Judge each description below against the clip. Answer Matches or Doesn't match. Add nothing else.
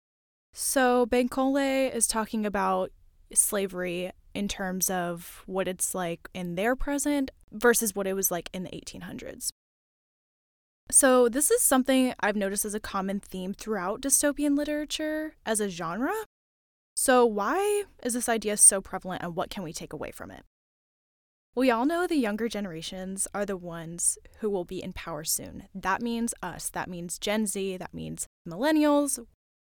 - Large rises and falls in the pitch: Matches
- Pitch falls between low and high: Doesn't match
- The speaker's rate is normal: Matches